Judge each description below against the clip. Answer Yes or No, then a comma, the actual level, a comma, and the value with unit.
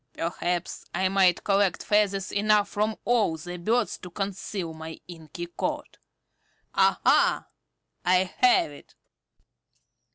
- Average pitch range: Yes, average, 3.0 semitones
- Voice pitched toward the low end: No, high, 190 Hz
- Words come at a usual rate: No, slow, 110 wpm